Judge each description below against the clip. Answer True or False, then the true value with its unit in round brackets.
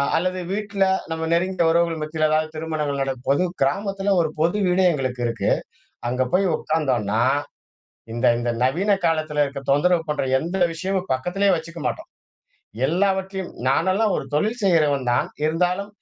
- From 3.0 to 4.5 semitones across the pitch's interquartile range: False (5.0 semitones)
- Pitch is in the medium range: True (165 Hz)